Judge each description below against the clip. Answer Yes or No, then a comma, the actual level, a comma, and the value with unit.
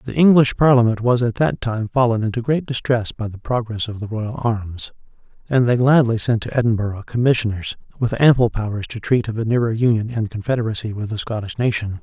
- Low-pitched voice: Yes, low, 115 Hz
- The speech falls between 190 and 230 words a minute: Yes, average, 200 wpm